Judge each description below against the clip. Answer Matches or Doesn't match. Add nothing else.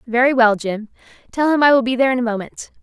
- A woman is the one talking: Matches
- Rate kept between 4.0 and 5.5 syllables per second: Doesn't match